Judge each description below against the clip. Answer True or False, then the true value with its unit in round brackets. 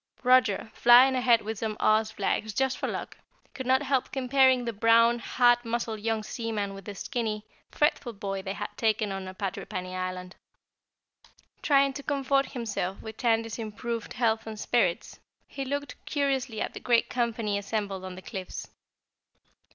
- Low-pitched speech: False (225 Hz)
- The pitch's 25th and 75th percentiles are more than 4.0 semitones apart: False (3.6 semitones)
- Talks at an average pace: True (160 wpm)